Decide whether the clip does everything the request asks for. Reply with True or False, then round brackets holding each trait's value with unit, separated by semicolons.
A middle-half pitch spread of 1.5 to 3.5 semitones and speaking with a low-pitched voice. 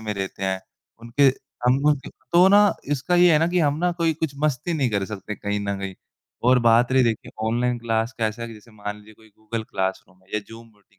False (5.2 semitones; 115 Hz)